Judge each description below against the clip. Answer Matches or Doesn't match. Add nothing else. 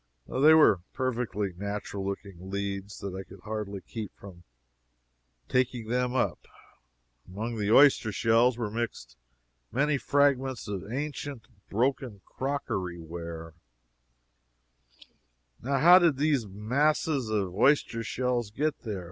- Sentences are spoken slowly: Matches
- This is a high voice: Doesn't match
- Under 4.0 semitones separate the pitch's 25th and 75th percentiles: Doesn't match